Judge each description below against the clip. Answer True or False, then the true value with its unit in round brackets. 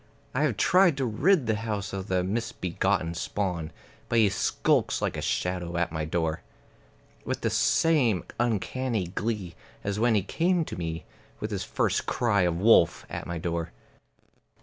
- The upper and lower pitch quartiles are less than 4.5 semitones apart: False (5.2 semitones)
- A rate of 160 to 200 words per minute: True (165 wpm)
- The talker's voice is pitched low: True (100 Hz)